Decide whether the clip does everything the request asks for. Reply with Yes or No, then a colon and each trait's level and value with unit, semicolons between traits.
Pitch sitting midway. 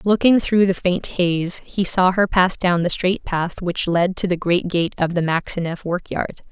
Yes: medium, 180 Hz